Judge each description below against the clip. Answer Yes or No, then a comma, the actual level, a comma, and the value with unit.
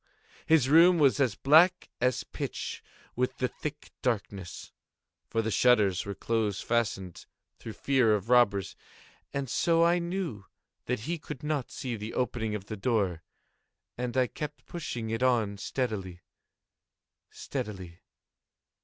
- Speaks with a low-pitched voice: Yes, low, 120 Hz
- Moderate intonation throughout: Yes, average, 5.0 semitones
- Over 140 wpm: No, slow, 135 wpm